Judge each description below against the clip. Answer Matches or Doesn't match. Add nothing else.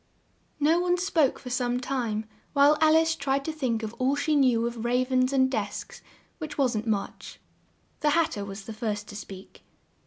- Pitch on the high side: Matches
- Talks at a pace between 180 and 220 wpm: Matches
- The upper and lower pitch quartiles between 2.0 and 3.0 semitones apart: Doesn't match